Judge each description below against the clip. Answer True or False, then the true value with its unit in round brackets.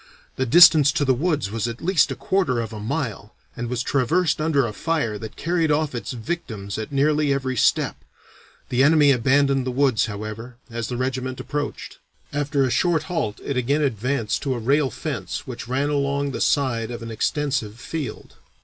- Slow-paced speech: False (185 wpm)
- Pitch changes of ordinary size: True (3.9 semitones)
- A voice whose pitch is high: False (135 Hz)